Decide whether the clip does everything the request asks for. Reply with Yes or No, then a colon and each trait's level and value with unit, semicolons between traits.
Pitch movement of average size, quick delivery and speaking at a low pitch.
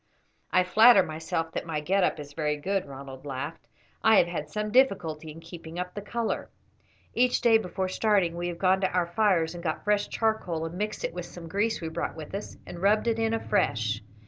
No: average, 4.4 semitones; fast, 215 wpm; medium, 175 Hz